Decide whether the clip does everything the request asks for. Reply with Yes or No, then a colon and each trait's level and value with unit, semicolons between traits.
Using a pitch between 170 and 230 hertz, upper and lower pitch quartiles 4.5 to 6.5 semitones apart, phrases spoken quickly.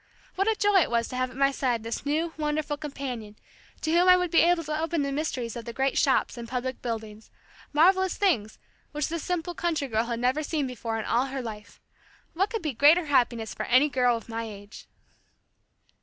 No: very high, 275 Hz; wide, 5.5 semitones; fast, 215 wpm